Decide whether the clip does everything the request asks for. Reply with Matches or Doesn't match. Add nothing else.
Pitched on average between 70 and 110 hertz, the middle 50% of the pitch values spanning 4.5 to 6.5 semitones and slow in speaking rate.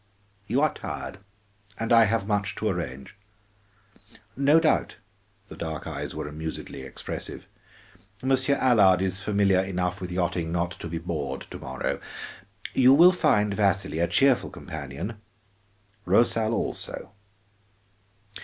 Matches